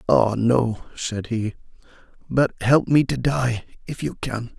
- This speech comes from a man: Yes, male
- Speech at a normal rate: Yes, average, 155 wpm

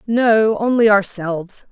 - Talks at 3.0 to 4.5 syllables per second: Yes, 3.9 syllables/s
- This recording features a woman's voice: Yes, female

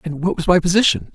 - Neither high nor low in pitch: Yes, medium, 175 Hz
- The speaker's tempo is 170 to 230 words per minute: No, fast, 260 wpm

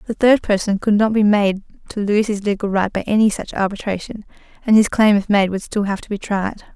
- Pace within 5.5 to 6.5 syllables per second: Yes, 5.6 syllables/s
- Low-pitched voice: No, high, 205 Hz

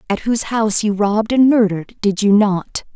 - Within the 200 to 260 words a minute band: Yes, fast, 205 wpm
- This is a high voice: Yes, high, 210 Hz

